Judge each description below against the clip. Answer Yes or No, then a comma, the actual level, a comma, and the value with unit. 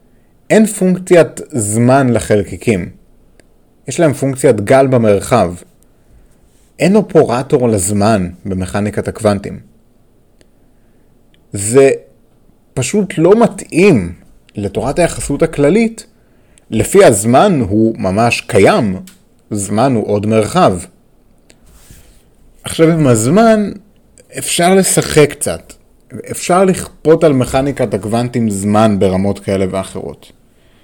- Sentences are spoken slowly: Yes, slow, 90 wpm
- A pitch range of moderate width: No, wide, 8.0 semitones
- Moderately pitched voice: No, low, 125 Hz